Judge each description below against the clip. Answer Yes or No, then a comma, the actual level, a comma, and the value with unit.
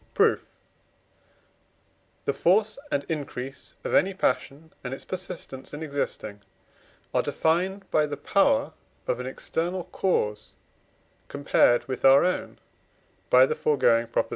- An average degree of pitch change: No, wide, 5.7 semitones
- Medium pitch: Yes, medium, 150 Hz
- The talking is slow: Yes, slow, 125 wpm